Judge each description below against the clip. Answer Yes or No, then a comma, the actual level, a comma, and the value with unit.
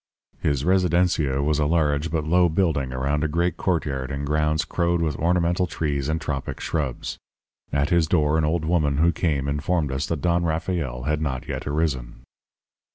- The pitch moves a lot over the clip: No, average, 3.0 semitones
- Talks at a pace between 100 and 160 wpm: No, average, 175 wpm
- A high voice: No, very low, 75 Hz